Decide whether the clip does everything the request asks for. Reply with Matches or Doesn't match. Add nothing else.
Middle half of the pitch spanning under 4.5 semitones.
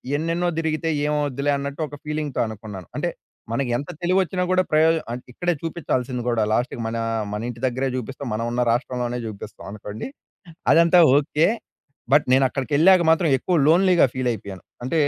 Doesn't match